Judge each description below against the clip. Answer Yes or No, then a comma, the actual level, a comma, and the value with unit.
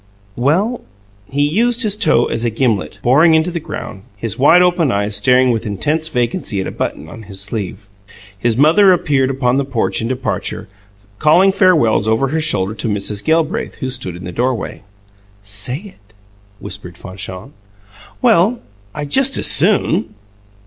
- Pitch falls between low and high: No, low, 130 Hz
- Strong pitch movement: Yes, wide, 7.8 semitones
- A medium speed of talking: Yes, average, 165 wpm